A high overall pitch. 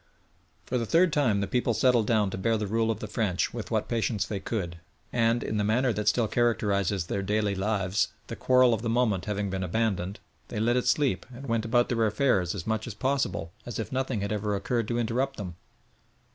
No: low, 110 Hz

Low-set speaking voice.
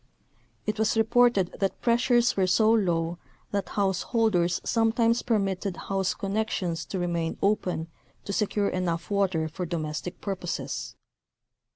No: high, 195 Hz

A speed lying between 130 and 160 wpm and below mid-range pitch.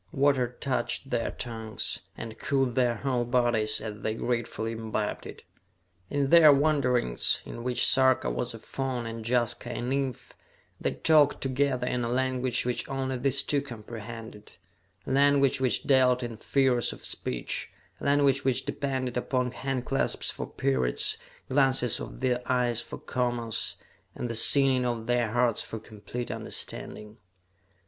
Yes: average, 150 wpm; low, 125 Hz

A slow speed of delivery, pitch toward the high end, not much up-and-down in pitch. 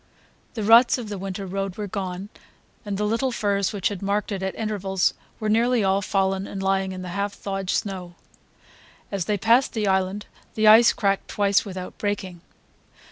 No: average, 180 wpm; high, 200 Hz; narrow, 1.7 semitones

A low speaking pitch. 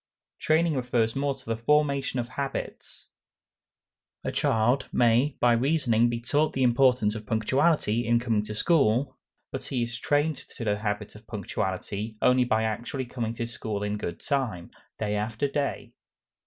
Yes: low, 120 Hz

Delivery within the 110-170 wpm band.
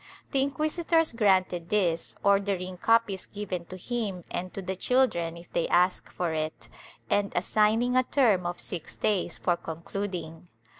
Yes: average, 155 wpm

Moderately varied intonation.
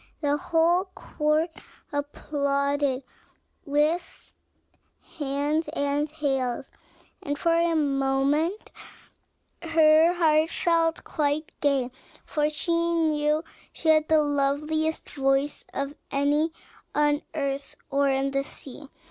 No: narrow, 2.2 semitones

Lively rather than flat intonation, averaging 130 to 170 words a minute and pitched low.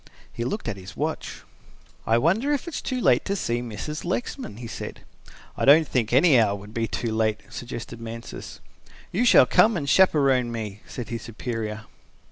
No: wide, 6.1 semitones; average, 185 wpm; low, 120 Hz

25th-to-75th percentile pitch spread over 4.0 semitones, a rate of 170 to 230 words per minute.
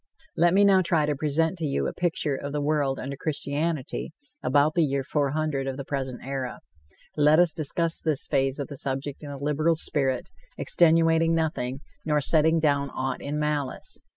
No: average, 2.7 semitones; average, 180 wpm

